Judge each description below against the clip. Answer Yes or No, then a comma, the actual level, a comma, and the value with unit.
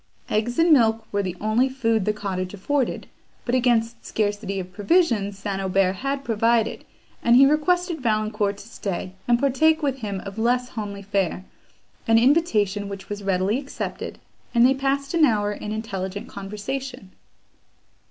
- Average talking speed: Yes, average, 155 wpm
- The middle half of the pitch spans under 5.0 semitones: Yes, average, 4.5 semitones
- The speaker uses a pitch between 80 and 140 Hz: No, high, 220 Hz